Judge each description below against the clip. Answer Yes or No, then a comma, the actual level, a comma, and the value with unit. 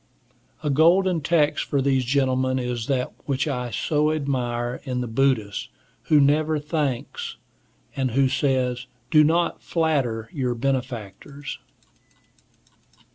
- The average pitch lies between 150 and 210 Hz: No, low, 135 Hz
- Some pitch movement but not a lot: Yes, average, 3.1 semitones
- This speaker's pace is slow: Yes, slow, 120 wpm